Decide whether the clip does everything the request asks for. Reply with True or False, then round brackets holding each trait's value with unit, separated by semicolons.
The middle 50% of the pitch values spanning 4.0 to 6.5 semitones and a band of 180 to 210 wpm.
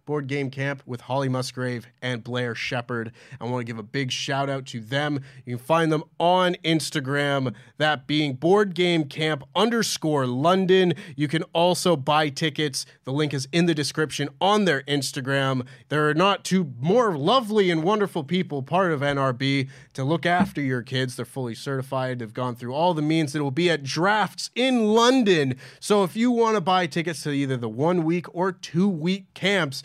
True (4.9 semitones; 190 wpm)